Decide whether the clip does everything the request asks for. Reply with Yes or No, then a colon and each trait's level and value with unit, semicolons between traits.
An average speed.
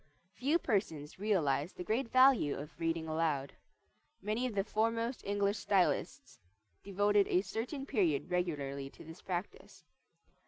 No: slow, 130 wpm